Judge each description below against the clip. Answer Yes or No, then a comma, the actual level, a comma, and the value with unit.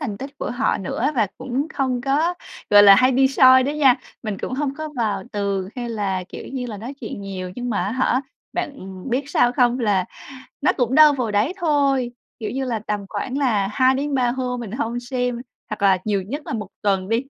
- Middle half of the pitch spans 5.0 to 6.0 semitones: No, average, 4.3 semitones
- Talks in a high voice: Yes, high, 245 Hz